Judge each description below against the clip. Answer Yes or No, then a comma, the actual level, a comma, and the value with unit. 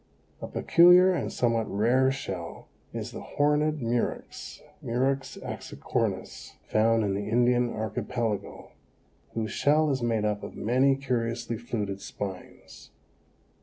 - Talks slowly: Yes, slow, 120 wpm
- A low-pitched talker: Yes, low, 120 Hz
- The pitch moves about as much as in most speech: Yes, average, 3.7 semitones